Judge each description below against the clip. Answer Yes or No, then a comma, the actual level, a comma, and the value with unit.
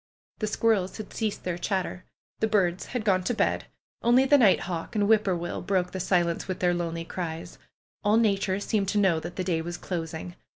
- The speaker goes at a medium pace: No, fast, 215 wpm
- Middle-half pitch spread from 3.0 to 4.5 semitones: Yes, average, 3.4 semitones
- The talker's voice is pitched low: No, medium, 185 Hz